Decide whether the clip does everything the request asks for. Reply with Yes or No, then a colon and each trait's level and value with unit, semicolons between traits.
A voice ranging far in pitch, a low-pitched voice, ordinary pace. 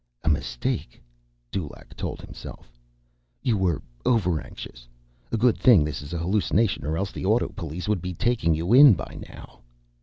Yes: wide, 5.7 semitones; very low, 90 Hz; average, 155 wpm